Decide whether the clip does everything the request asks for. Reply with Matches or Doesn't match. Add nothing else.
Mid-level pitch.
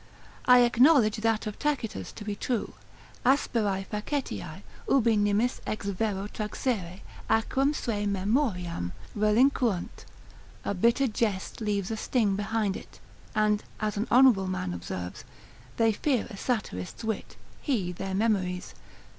Doesn't match